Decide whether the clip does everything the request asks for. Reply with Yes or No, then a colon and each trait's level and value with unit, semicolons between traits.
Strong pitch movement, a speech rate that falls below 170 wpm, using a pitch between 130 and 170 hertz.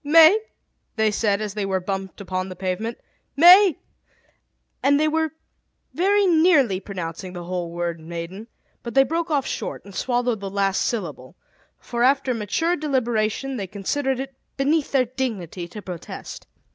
No: wide, 6.8 semitones; average, 160 wpm; high, 225 Hz